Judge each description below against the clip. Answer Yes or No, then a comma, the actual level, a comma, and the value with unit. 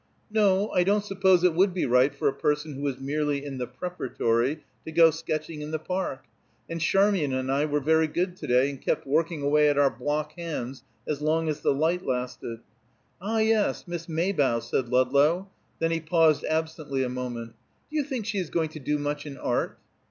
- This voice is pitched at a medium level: Yes, medium, 155 Hz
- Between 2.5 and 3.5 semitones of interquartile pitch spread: No, average, 4.0 semitones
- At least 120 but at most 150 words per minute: No, fast, 205 wpm